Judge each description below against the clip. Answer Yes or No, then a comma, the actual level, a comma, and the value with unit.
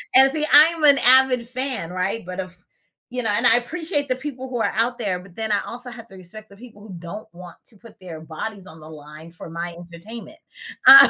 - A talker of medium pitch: No, high, 220 Hz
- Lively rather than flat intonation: Yes, wide, 6.1 semitones